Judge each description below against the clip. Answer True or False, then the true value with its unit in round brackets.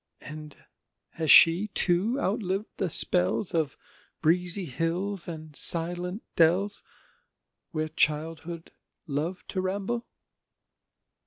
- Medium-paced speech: False (95 wpm)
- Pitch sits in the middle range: True (170 Hz)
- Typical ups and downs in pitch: True (3.2 semitones)